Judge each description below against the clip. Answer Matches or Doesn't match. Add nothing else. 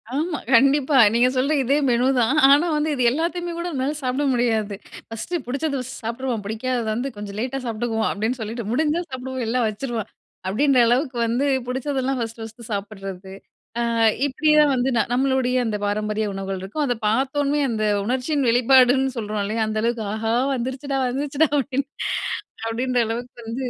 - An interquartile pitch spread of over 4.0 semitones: Doesn't match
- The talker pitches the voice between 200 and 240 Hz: Doesn't match